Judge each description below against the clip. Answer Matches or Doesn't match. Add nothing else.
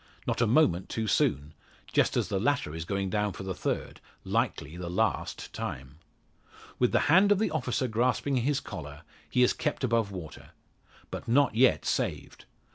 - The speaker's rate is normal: Matches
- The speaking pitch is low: Matches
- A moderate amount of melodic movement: Doesn't match